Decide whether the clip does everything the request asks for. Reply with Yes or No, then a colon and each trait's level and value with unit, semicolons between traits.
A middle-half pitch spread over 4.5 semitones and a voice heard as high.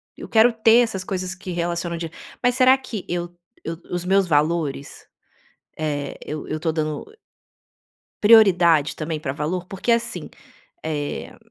No: average, 5.0 semitones; medium, 175 Hz